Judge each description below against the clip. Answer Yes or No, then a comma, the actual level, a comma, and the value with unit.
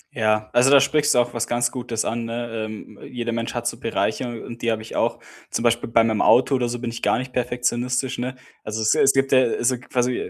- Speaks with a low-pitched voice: Yes, low, 120 Hz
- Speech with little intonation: Yes, narrow, 1.6 semitones